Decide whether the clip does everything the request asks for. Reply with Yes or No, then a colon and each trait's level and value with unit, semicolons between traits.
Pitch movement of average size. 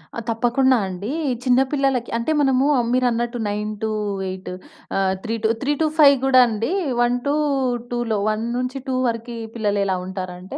Yes: average, 3.7 semitones